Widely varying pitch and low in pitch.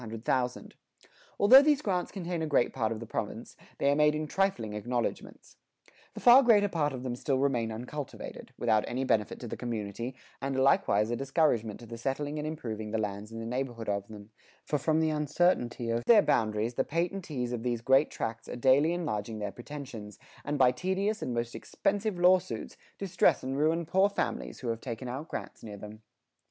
Yes: wide, 5.9 semitones; low, 130 Hz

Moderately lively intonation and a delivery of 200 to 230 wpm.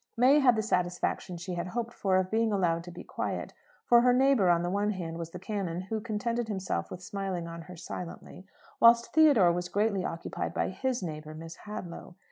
Yes: average, 4.6 semitones; fast, 205 wpm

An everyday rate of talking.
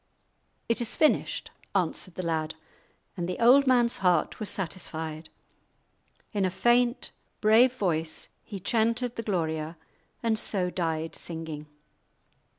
No: slow, 125 wpm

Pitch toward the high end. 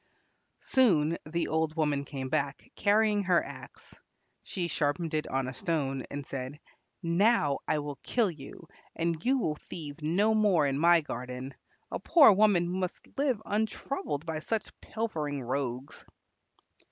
No: medium, 160 Hz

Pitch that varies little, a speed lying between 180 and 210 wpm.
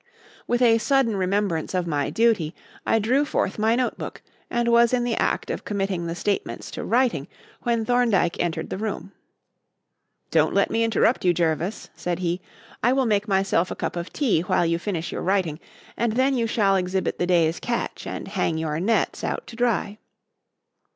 No: average, 5.0 semitones; average, 185 wpm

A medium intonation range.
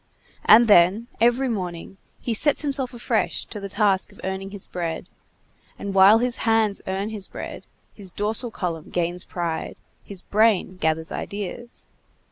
Yes: average, 3.6 semitones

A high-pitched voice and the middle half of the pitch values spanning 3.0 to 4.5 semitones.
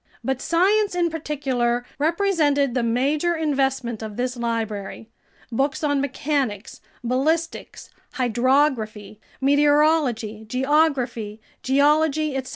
Yes: very high, 270 Hz; average, 4.1 semitones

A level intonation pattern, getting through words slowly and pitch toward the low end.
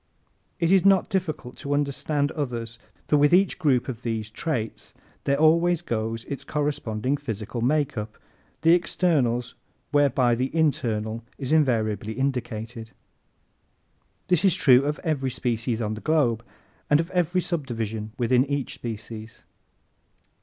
No: average, 5.1 semitones; slow, 130 wpm; low, 130 Hz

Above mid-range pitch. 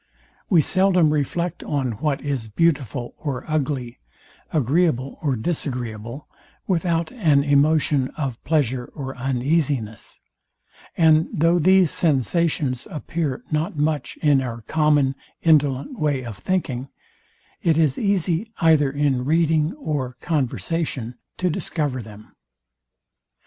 No: medium, 150 Hz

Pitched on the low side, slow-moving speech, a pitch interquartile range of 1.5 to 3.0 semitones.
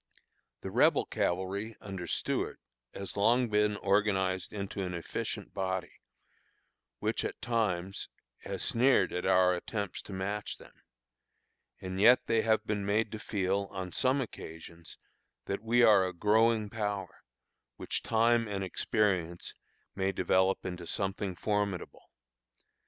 Yes: low, 100 Hz; slow, 130 wpm; narrow, 2.6 semitones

